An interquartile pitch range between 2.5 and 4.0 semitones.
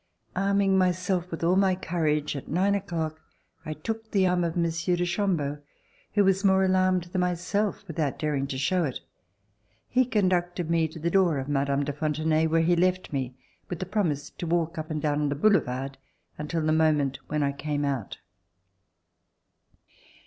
Yes: average, 3.7 semitones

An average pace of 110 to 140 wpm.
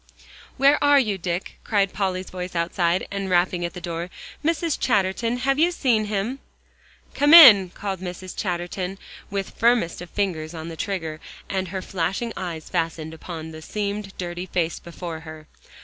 No: average, 165 wpm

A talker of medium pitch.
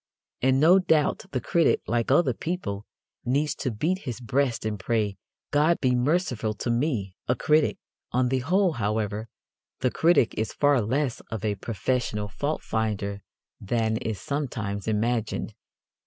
No: low, 120 Hz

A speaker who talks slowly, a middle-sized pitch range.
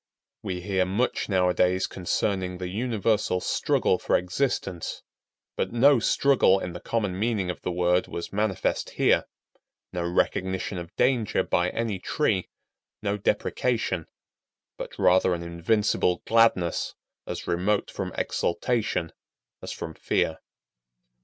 Yes: slow, 125 wpm; average, 3.5 semitones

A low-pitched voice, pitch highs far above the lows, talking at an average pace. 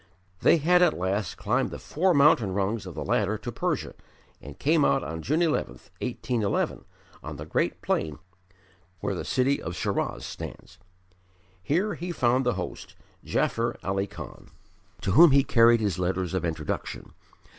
Yes: low, 115 Hz; wide, 7.6 semitones; average, 160 wpm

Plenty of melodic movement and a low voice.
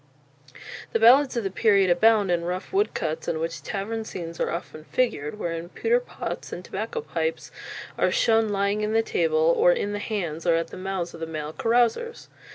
No: wide, 5.7 semitones; high, 205 Hz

